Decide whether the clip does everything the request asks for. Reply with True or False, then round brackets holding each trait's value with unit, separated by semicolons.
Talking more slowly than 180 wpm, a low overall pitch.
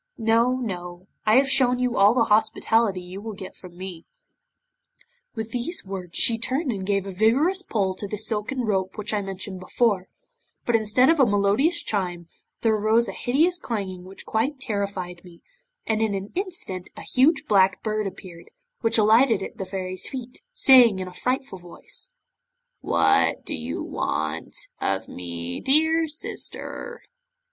False (165 wpm; 215 Hz)